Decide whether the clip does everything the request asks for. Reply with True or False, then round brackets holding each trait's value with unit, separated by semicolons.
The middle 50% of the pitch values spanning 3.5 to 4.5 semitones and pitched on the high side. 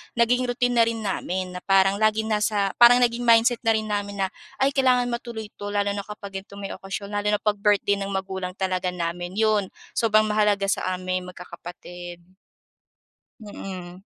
False (2.8 semitones; 205 Hz)